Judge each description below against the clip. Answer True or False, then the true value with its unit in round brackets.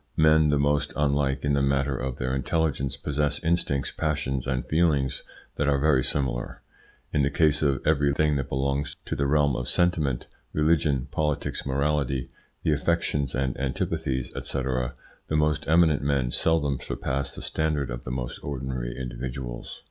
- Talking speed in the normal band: True (160 wpm)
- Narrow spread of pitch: True (2.3 semitones)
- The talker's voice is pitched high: False (70 Hz)